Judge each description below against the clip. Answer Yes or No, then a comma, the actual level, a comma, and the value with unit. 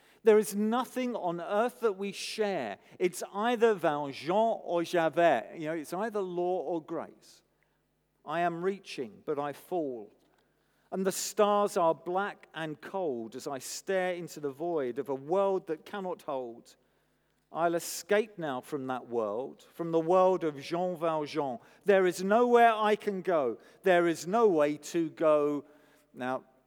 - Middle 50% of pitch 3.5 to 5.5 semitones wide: Yes, average, 4.5 semitones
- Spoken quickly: No, average, 160 wpm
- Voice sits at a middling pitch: Yes, medium, 175 Hz